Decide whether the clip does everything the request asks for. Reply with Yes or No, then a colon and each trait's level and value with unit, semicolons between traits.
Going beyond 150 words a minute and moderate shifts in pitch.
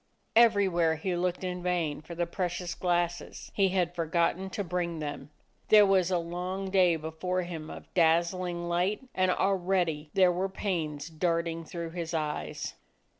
No: average, 160 wpm; narrow, 1.9 semitones